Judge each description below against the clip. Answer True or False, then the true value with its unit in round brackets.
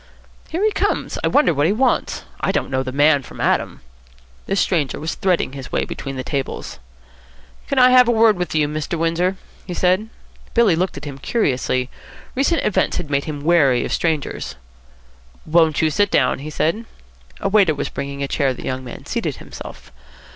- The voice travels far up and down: True (5.8 semitones)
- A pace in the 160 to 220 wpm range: True (190 wpm)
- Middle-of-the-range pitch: True (160 Hz)